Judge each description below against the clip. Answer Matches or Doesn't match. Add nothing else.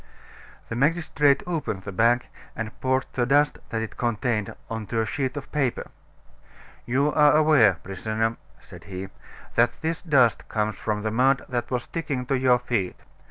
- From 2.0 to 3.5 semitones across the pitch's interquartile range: Doesn't match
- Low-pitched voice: Matches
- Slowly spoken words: Doesn't match